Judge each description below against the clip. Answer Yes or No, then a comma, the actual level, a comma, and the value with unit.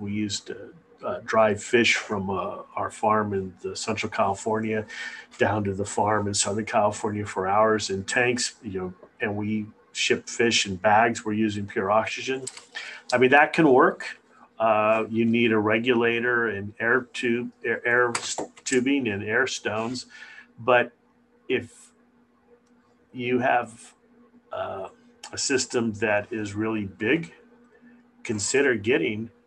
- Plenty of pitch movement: No, average, 3.2 semitones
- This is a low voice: Yes, low, 115 Hz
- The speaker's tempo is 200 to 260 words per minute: No, average, 140 wpm